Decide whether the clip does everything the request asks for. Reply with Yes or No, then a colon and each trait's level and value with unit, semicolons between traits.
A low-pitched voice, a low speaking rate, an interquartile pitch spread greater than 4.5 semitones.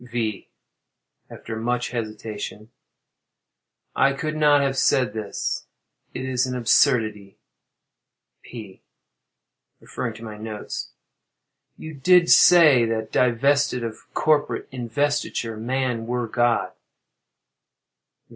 No: low, 120 Hz; slow, 100 wpm; average, 3.5 semitones